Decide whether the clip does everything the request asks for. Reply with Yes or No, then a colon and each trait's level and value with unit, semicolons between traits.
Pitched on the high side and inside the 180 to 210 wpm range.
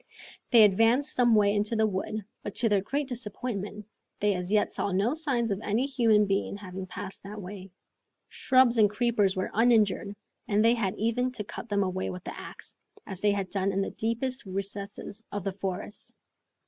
Yes: high, 210 Hz; average, 190 wpm